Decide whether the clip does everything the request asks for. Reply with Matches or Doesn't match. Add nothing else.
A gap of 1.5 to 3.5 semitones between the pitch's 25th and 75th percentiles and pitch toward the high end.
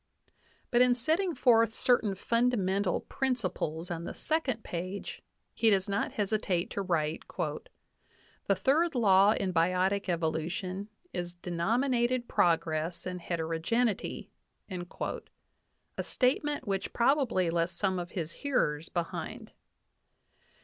Doesn't match